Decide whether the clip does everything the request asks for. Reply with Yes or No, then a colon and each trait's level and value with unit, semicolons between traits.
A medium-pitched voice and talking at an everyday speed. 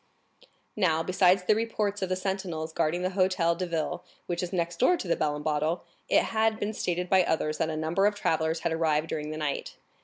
No: medium, 175 Hz; fast, 220 wpm